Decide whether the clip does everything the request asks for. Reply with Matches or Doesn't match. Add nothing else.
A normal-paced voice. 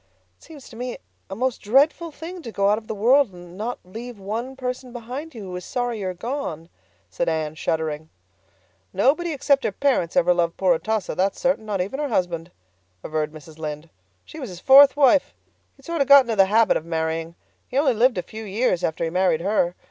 Doesn't match